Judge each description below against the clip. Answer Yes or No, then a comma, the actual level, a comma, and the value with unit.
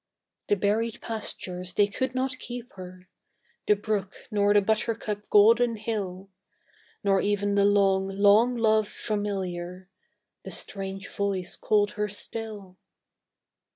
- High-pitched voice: Yes, high, 205 Hz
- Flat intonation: Yes, narrow, 2.1 semitones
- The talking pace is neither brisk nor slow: No, slow, 120 wpm